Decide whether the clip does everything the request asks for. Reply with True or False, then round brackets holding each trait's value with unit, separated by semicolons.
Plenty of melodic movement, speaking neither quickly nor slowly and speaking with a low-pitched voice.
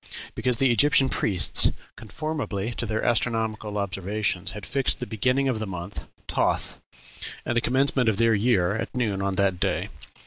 False (3.8 semitones; 165 wpm; 110 Hz)